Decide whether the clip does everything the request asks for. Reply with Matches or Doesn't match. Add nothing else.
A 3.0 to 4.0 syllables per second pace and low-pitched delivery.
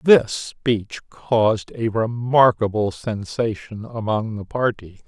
Matches